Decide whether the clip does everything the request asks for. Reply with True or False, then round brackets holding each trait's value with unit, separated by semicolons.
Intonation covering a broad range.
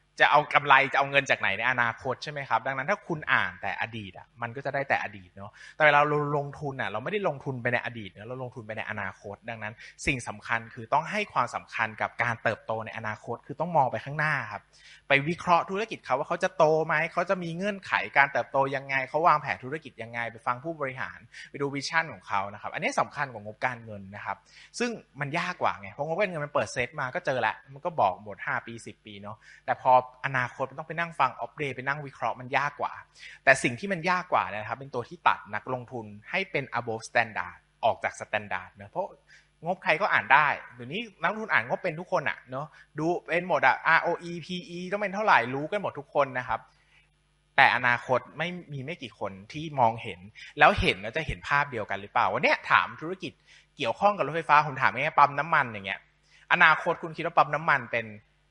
True (6.0 semitones)